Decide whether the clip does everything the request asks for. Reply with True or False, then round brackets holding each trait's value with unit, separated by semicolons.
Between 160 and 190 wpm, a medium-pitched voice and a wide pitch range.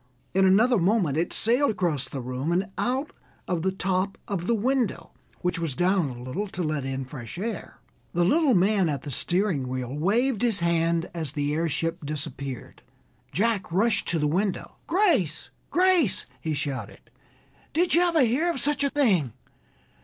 True (170 wpm; 180 Hz; 7.3 semitones)